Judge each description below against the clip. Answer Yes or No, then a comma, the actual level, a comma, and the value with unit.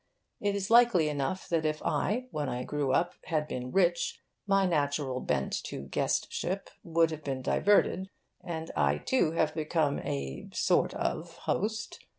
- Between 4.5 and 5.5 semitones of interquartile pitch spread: Yes, average, 5.1 semitones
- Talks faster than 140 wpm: Yes, average, 160 wpm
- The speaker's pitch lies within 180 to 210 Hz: No, medium, 155 Hz